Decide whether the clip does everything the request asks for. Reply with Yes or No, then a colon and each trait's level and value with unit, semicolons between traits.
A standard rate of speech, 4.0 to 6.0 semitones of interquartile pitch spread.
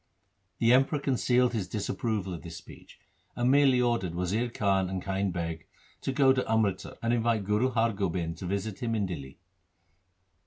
Yes: average, 170 wpm; average, 4.7 semitones